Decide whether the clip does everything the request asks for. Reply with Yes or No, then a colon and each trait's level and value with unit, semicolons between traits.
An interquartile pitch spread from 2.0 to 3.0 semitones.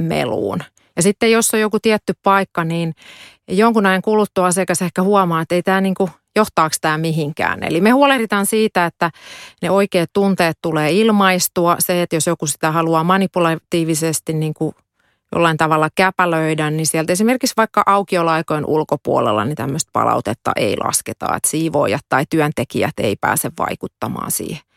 No: average, 3.6 semitones